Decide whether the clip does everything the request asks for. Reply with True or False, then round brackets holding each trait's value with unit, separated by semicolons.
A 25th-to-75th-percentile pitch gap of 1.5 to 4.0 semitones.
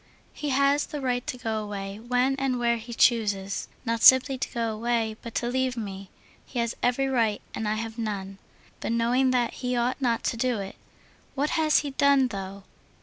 True (2.9 semitones)